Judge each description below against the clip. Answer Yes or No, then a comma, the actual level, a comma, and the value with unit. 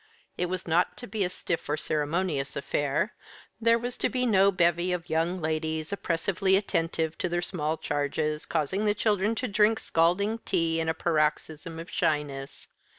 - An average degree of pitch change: Yes, average, 3.8 semitones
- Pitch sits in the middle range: Yes, medium, 170 Hz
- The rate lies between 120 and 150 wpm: No, average, 170 wpm